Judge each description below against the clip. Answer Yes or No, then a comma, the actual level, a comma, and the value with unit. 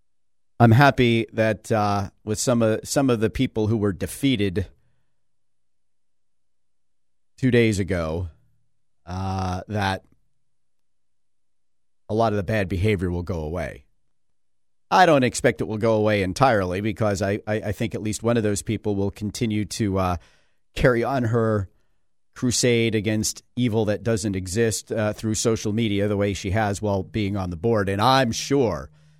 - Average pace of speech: Yes, average, 155 wpm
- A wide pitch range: No, average, 3.9 semitones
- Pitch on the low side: Yes, low, 105 Hz